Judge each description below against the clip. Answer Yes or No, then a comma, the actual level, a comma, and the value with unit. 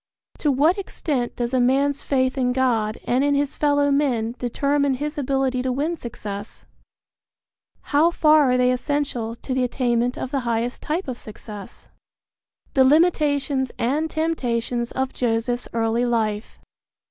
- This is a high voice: Yes, very high, 260 Hz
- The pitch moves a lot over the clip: No, average, 3.2 semitones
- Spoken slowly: No, average, 150 wpm